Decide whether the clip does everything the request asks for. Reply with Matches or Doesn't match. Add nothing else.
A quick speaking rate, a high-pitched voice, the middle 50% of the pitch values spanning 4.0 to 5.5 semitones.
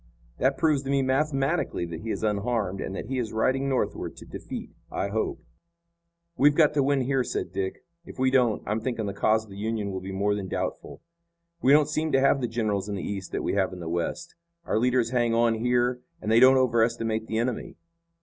Doesn't match